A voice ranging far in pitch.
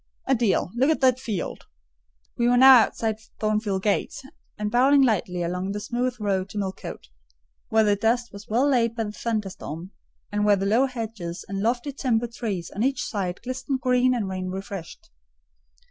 No: average, 4.0 semitones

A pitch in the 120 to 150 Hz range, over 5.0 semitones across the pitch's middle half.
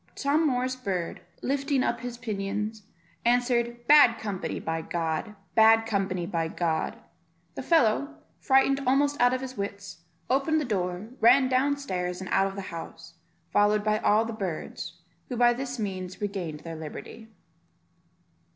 No: high, 220 Hz; wide, 5.4 semitones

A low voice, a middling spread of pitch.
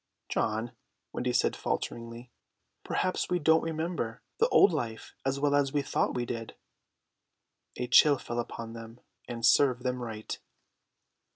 Yes: low, 125 Hz; average, 3.9 semitones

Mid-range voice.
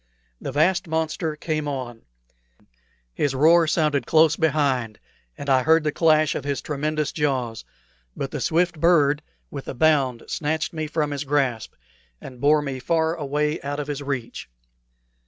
Yes: medium, 150 Hz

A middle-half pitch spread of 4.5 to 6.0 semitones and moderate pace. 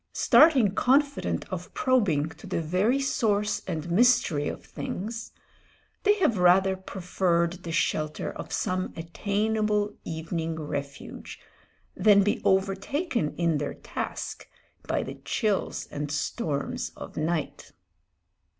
No: average, 5.0 semitones; slow, 115 wpm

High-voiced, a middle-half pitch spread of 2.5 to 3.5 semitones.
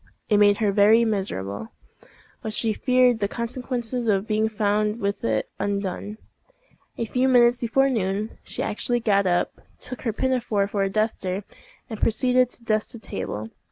Yes: high, 215 Hz; average, 3.0 semitones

